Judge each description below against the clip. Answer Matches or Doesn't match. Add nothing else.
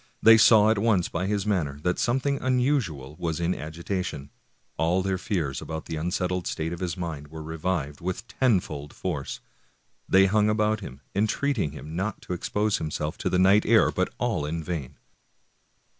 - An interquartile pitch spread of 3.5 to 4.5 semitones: Doesn't match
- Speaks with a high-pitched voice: Doesn't match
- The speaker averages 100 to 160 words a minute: Doesn't match